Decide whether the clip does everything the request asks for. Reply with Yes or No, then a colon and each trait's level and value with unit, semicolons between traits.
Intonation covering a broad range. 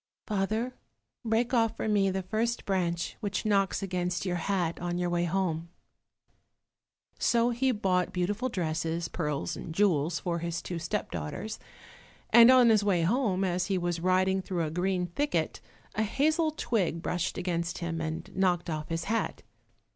No: average, 4.0 semitones